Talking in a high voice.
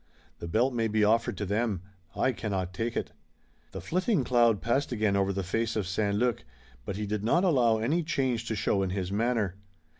No: low, 110 Hz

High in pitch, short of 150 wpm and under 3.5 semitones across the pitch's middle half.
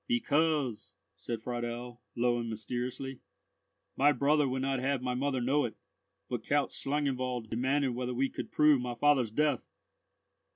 No: low, 130 Hz; slow, 135 wpm; average, 2.7 semitones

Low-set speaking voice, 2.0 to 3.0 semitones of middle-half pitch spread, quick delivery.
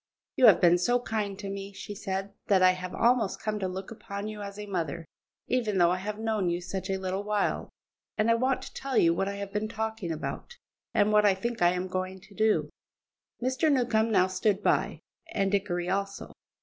No: high, 200 Hz; average, 2.7 semitones; fast, 215 wpm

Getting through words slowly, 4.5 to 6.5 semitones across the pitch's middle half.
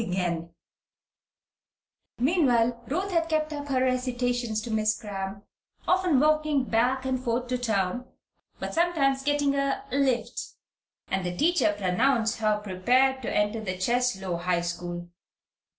Yes: slow, 130 wpm; average, 5.0 semitones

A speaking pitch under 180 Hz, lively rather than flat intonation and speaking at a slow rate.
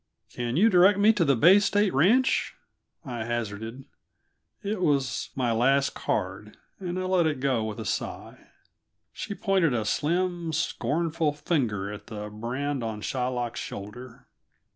No: low, 135 Hz; wide, 7.4 semitones; average, 145 wpm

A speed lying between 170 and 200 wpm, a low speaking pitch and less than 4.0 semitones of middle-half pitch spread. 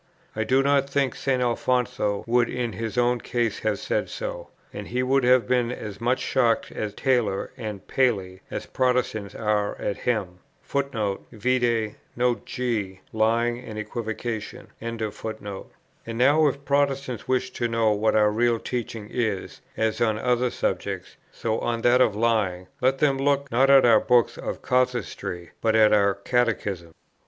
No: average, 155 wpm; low, 115 Hz; average, 2.9 semitones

